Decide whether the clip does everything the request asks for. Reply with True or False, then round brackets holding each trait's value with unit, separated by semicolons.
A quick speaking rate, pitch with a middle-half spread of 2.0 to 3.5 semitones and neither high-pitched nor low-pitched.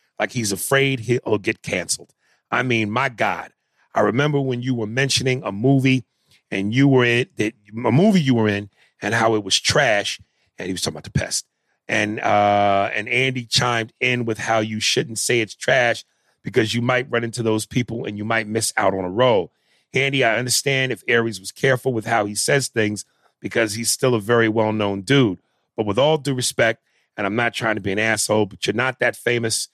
False (210 wpm; 3.1 semitones; 115 Hz)